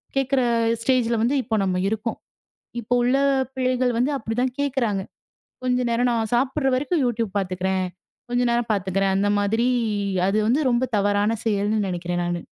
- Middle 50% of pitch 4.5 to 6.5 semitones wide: No, average, 4.1 semitones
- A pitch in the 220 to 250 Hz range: Yes, high, 230 Hz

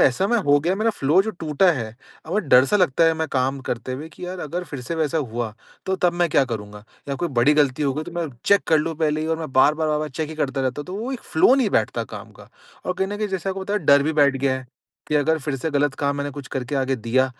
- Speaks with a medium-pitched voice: Yes, medium, 150 Hz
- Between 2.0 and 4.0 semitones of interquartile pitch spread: No, average, 4.4 semitones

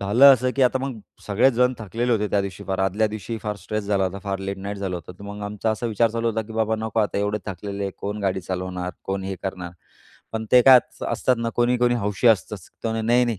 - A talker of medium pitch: No, low, 105 Hz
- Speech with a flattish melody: No, average, 3.0 semitones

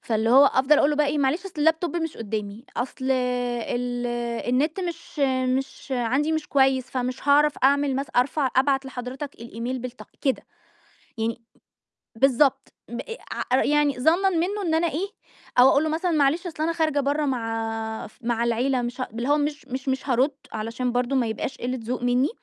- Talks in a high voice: Yes, very high, 270 Hz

